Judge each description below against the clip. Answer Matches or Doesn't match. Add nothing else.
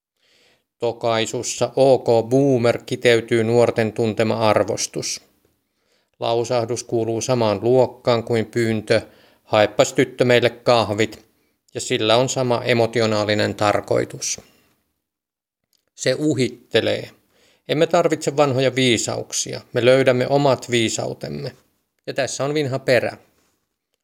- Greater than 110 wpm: Doesn't match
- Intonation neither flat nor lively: Doesn't match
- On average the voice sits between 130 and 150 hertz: Doesn't match